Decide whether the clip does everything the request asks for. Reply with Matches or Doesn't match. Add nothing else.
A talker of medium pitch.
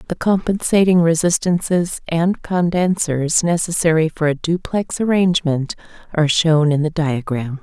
Matches